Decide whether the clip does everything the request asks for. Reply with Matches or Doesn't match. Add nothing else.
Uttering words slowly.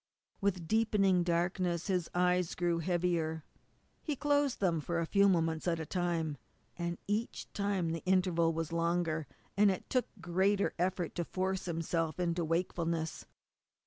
Doesn't match